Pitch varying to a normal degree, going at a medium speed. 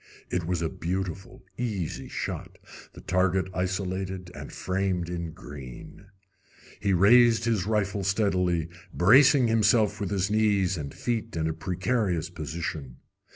No: average, 3.3 semitones; slow, 125 wpm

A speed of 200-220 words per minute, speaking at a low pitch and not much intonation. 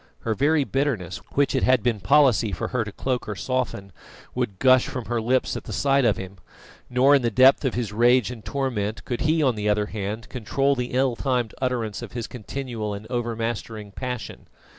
No: fast, 205 wpm; low, 120 Hz; average, 3.4 semitones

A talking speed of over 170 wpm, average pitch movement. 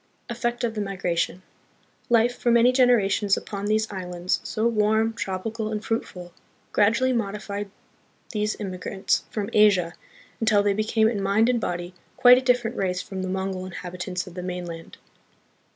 No: average, 160 wpm; average, 3.3 semitones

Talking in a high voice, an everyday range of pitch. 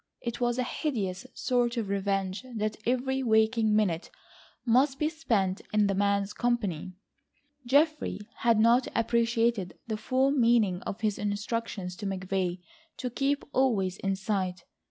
Yes: high, 220 Hz; average, 3.8 semitones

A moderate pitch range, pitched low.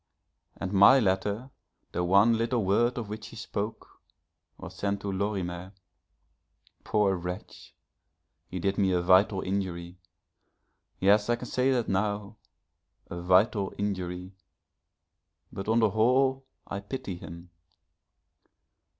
Yes: average, 3.0 semitones; low, 100 Hz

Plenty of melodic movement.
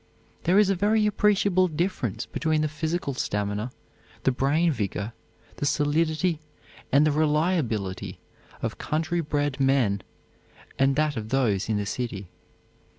Yes: wide, 5.9 semitones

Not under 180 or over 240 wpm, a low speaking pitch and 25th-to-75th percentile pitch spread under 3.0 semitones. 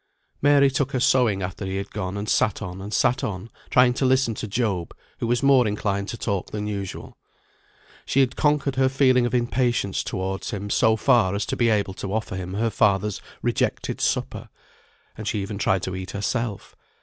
No: average, 195 wpm; low, 105 Hz; average, 4.2 semitones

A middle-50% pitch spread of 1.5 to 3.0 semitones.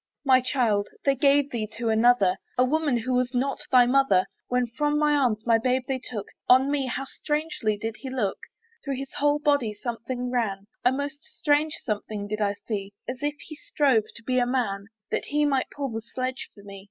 No: average, 4.0 semitones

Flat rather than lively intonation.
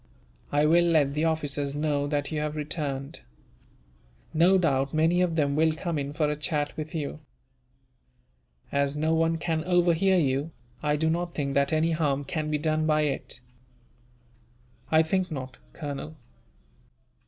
Yes: narrow, 2.1 semitones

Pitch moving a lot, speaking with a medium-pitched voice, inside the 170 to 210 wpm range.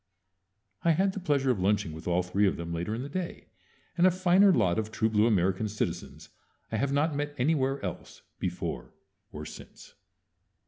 No: wide, 8.8 semitones; low, 125 Hz; average, 185 wpm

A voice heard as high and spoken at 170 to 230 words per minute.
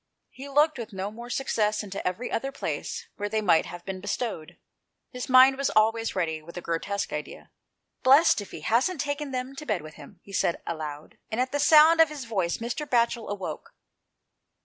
Yes: high, 225 Hz; average, 195 wpm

